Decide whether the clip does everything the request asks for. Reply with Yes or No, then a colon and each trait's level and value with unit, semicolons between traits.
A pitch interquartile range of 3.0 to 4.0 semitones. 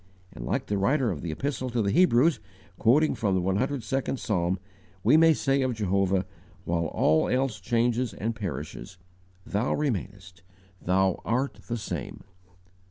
No: wide, 5.6 semitones